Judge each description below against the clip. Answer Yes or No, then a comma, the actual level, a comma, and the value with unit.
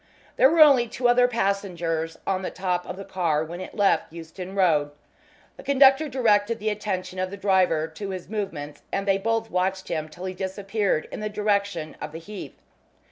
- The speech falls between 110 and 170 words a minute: No, average, 190 wpm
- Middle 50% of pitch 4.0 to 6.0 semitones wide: No, average, 3.2 semitones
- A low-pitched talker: No, high, 195 Hz